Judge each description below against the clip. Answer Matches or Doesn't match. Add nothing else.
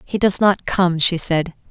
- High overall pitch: Doesn't match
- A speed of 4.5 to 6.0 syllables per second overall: Doesn't match